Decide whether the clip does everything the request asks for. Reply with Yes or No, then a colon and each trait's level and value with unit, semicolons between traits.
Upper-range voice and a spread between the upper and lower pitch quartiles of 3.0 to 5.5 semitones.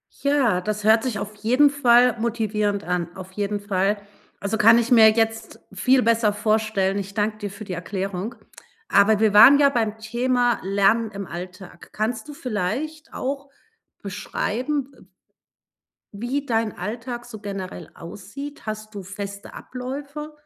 Yes: high, 220 Hz; average, 3.5 semitones